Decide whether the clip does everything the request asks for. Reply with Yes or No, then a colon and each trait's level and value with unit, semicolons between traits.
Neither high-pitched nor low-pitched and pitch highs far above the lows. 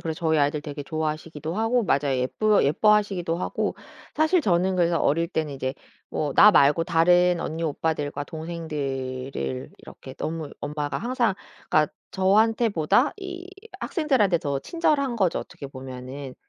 Yes: medium, 165 Hz; wide, 6.3 semitones